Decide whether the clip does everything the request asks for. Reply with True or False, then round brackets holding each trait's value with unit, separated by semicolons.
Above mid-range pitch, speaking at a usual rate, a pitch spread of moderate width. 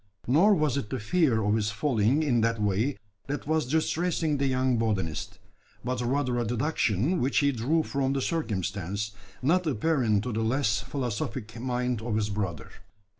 False (125 Hz; 170 wpm; 5.0 semitones)